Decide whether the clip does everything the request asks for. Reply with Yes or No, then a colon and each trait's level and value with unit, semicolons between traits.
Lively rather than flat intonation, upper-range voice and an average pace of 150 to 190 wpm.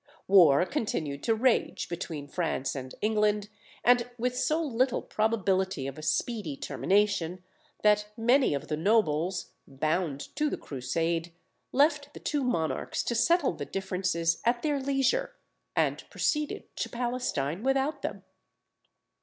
No: wide, 7.3 semitones; high, 210 Hz; slow, 135 wpm